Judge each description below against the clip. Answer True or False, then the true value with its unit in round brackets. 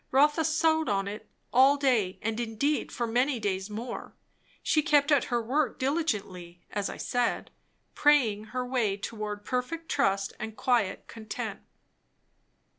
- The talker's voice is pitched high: True (240 Hz)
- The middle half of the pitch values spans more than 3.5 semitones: True (5.3 semitones)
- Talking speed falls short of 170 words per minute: True (140 wpm)